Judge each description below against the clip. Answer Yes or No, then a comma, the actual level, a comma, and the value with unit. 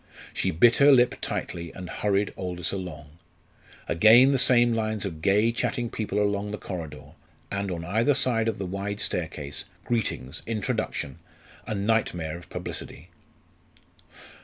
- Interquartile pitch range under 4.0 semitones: No, average, 4.4 semitones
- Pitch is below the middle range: Yes, low, 100 Hz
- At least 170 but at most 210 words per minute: No, average, 140 wpm